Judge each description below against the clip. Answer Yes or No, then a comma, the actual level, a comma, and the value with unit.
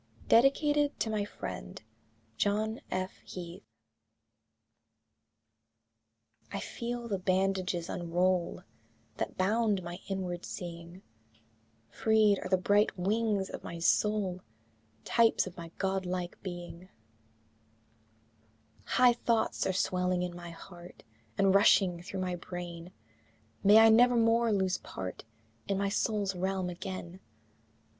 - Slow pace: Yes, slow, 120 wpm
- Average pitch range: Yes, average, 3.0 semitones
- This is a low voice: No, high, 190 Hz